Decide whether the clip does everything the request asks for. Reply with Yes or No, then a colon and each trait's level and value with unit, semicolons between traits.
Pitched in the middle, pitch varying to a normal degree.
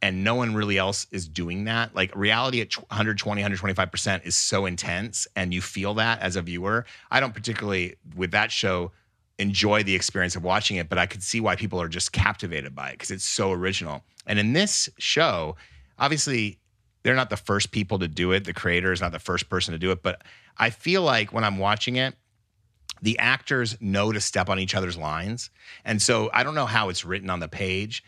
No: low, 100 Hz; average, 3.1 semitones